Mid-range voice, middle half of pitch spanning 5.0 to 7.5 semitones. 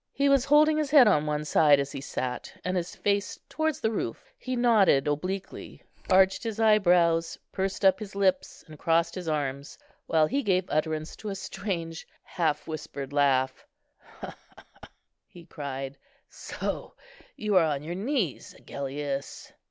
Yes: medium, 170 Hz; wide, 5.6 semitones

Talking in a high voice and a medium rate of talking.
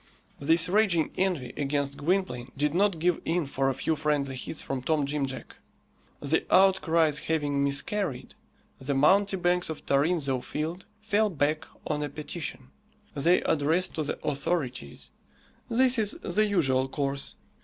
No: medium, 155 Hz; average, 145 wpm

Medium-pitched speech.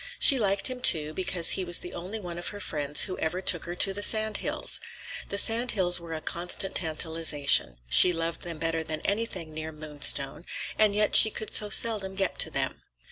Yes: medium, 175 Hz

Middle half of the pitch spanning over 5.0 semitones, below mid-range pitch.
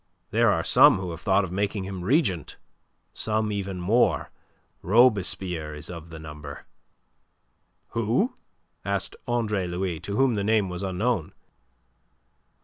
No: average, 3.7 semitones; very low, 95 Hz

